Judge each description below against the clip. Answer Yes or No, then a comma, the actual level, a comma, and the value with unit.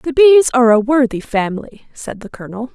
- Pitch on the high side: Yes, very high, 250 Hz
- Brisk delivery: No, average, 195 wpm